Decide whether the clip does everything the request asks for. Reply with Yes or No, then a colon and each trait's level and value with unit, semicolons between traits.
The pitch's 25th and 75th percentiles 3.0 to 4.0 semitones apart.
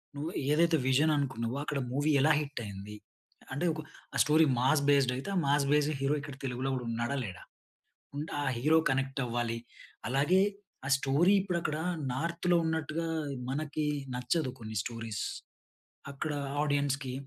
Yes: average, 3.5 semitones